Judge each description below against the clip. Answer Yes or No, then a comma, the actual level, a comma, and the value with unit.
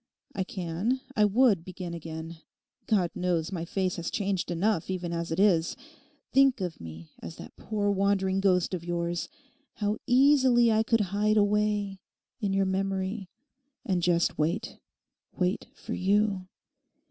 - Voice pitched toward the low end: No, high, 190 Hz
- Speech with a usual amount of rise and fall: Yes, average, 3.3 semitones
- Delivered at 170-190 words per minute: No, average, 145 wpm